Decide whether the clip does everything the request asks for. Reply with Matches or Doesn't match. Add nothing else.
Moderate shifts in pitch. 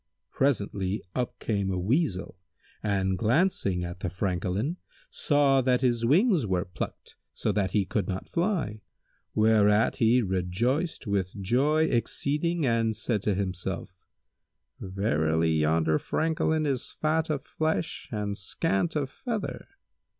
Doesn't match